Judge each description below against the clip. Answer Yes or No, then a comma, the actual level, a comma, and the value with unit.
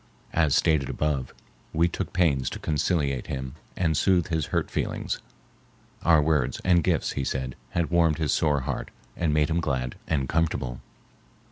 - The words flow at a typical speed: Yes, average, 160 wpm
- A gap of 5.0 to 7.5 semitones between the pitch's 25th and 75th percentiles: No, average, 3.7 semitones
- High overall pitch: No, very low, 75 Hz